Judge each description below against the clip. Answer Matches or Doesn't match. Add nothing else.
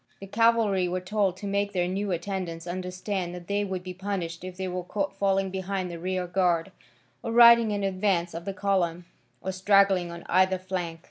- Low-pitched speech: Doesn't match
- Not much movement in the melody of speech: Matches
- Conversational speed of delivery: Matches